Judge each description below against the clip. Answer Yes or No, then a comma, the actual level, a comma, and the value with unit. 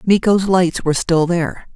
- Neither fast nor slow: Yes, average, 170 wpm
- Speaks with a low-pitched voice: No, medium, 180 Hz